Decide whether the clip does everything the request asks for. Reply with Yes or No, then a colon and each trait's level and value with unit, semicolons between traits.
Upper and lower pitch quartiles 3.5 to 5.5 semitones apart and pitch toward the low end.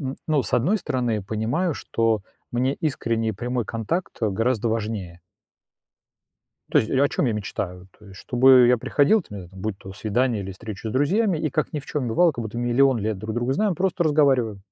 Yes: average, 4.5 semitones; low, 120 Hz